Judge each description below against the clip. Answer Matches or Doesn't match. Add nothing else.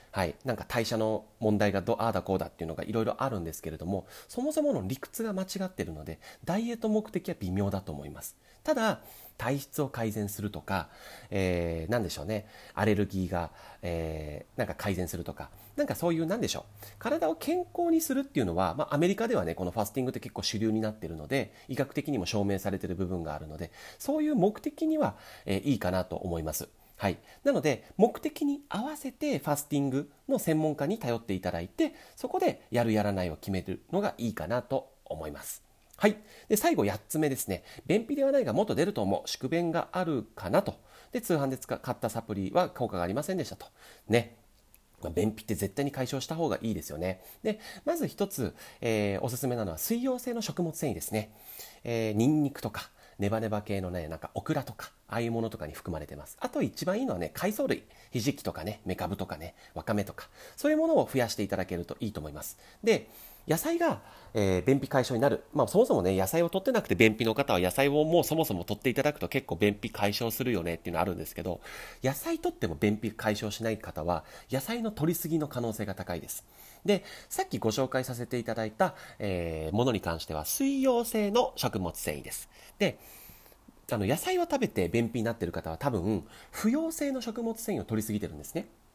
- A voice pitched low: Matches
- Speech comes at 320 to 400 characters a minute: Doesn't match